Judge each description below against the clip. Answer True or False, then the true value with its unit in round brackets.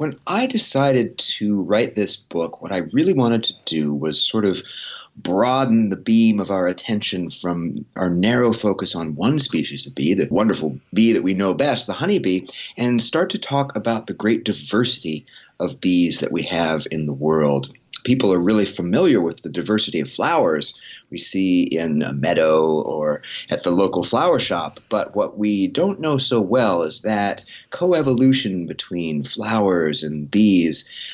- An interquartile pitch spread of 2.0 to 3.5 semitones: False (5.5 semitones)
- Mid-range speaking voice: False (100 Hz)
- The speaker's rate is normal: True (175 wpm)